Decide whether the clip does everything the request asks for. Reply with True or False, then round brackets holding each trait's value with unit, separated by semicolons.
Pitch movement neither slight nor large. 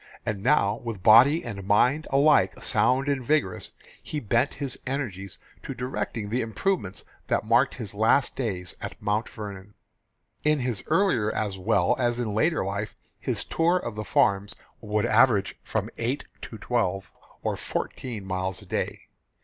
True (4.6 semitones)